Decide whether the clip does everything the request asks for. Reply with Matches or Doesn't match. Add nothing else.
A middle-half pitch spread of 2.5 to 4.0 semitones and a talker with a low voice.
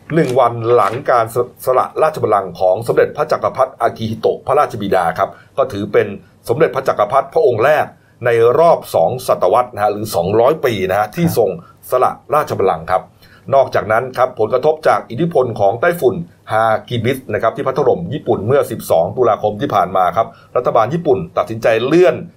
Matches